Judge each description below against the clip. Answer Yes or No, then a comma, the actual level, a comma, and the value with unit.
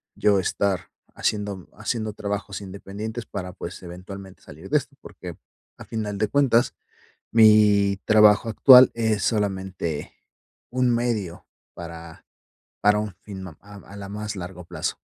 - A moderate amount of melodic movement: No, narrow, 2.2 semitones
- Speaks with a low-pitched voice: Yes, low, 100 Hz